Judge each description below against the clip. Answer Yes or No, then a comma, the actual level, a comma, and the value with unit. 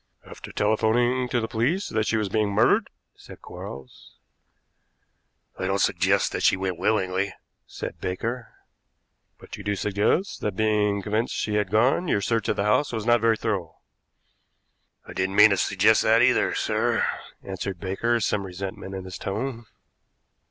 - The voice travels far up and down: No, average, 2.9 semitones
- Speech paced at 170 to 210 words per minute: No, average, 160 wpm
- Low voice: Yes, low, 105 Hz